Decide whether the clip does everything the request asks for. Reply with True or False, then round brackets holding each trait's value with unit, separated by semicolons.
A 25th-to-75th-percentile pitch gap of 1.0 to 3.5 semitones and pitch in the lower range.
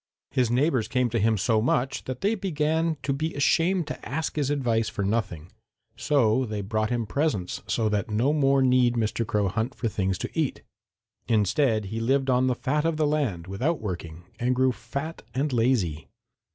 False (4.8 semitones; 125 Hz)